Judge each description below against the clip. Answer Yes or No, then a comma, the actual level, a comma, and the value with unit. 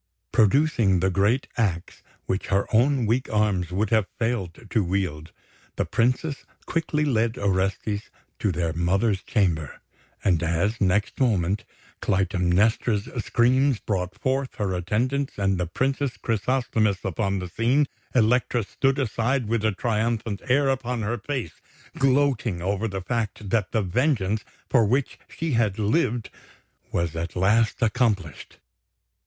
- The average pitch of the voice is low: Yes, low, 110 Hz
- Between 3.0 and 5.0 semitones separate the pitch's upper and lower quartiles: Yes, average, 4.5 semitones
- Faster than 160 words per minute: No, slow, 135 wpm